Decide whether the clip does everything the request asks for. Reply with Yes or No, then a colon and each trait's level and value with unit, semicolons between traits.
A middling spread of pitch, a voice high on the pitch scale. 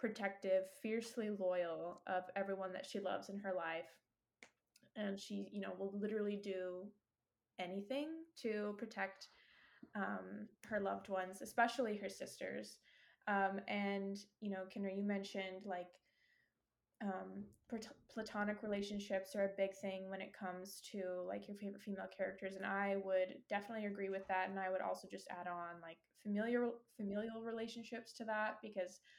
No: narrow, 2.2 semitones; high, 200 Hz